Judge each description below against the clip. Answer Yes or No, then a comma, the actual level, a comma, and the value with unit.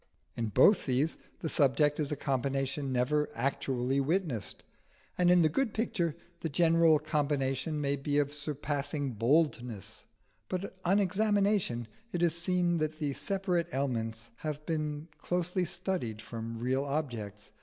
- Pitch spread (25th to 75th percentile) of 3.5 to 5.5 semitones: Yes, average, 4.3 semitones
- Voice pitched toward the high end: No, medium, 150 Hz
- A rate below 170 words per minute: Yes, average, 140 wpm